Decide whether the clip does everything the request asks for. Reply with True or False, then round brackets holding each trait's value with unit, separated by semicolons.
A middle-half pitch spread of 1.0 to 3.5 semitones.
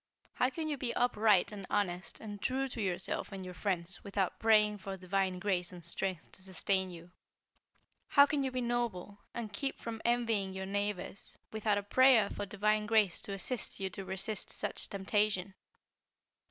True (2.9 semitones)